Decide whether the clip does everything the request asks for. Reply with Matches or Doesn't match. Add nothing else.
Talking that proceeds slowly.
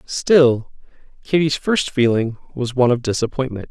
Matches